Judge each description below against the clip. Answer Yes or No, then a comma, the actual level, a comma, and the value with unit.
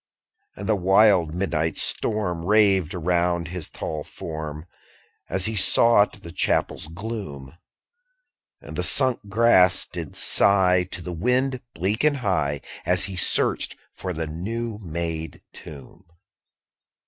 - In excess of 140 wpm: No, slow, 135 wpm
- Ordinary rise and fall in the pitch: Yes, average, 4.2 semitones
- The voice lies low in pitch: Yes, very low, 90 Hz